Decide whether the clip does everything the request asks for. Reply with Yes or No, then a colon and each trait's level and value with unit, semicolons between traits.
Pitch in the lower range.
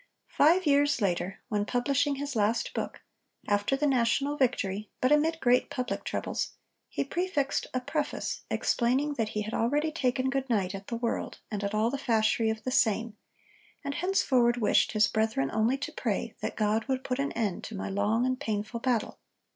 No: high, 240 Hz